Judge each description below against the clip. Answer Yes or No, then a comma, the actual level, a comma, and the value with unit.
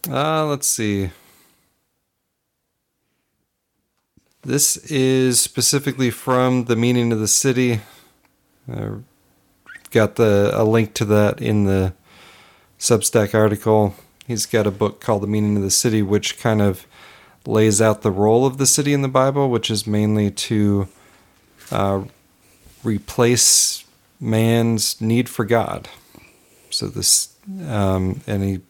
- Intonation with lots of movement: No, average, 3.5 semitones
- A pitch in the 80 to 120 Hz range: Yes, low, 110 Hz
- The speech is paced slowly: Yes, slow, 130 wpm